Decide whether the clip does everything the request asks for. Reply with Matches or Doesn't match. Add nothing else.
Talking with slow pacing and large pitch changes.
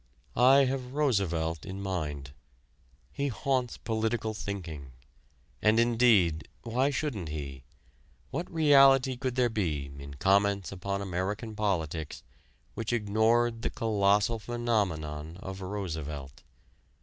Matches